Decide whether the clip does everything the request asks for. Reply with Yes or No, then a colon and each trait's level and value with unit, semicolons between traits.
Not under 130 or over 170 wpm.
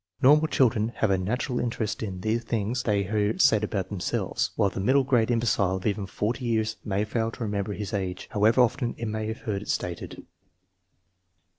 No: average, 200 wpm